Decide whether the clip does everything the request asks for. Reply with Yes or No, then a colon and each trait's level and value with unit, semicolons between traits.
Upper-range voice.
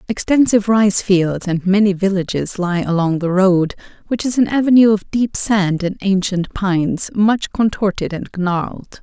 Yes: high, 195 Hz